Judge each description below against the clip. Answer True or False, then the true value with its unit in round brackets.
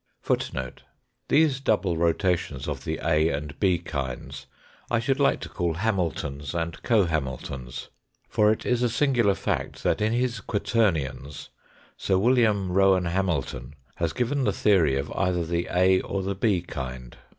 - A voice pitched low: True (90 Hz)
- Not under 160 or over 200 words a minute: False (150 wpm)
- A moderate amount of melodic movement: False (6.0 semitones)